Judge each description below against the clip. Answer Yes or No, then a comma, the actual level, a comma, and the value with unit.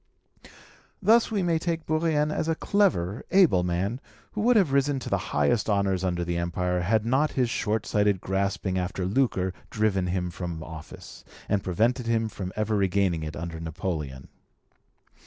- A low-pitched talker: Yes, low, 100 Hz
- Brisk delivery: No, average, 165 wpm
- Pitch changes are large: Yes, wide, 7.1 semitones